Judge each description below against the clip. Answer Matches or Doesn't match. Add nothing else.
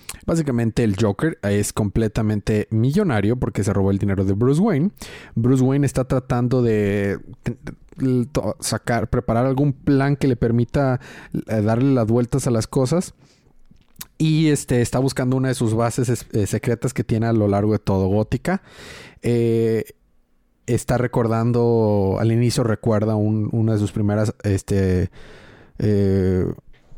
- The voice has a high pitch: Doesn't match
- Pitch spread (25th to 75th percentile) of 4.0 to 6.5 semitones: Doesn't match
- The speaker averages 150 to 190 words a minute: Doesn't match